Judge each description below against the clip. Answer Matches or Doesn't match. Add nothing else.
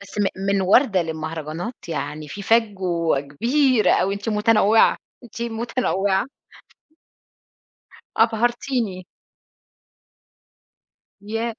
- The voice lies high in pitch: Matches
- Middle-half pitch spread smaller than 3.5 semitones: Doesn't match